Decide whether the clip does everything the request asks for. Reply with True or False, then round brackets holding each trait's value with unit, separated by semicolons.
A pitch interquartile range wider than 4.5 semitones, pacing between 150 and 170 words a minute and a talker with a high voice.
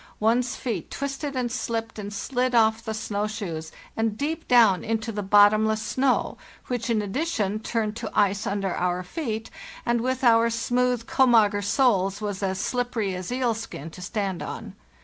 False (3.2 semitones; 165 wpm; 220 Hz)